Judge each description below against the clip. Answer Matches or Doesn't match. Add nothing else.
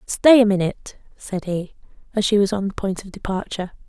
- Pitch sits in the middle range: Doesn't match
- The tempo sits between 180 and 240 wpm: Matches